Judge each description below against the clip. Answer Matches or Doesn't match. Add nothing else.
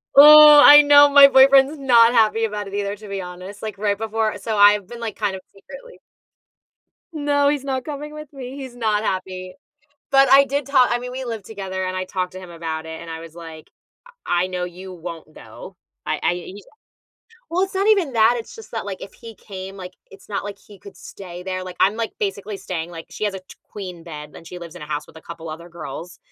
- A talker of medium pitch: Doesn't match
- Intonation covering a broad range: Matches